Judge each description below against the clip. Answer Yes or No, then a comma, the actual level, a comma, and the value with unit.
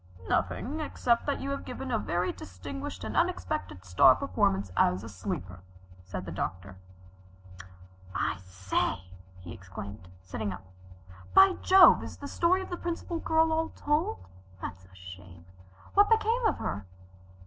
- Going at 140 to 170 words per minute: Yes, average, 150 wpm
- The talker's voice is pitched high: No, low, 100 Hz